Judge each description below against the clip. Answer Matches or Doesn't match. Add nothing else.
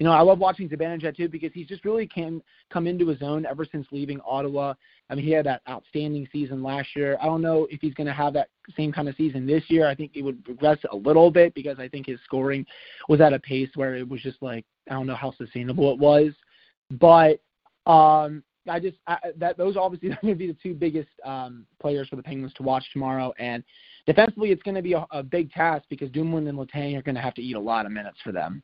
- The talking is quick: Matches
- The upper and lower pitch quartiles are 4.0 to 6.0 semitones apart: Doesn't match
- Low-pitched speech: Doesn't match